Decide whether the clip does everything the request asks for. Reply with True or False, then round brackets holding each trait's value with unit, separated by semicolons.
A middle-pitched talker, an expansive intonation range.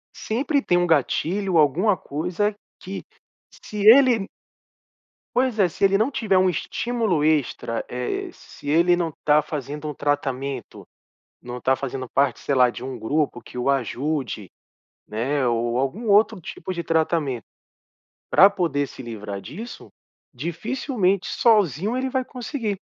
True (160 Hz; 7.4 semitones)